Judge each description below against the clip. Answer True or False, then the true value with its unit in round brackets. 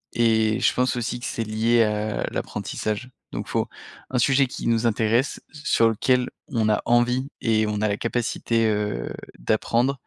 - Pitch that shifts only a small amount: True (2.3 semitones)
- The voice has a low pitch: True (115 Hz)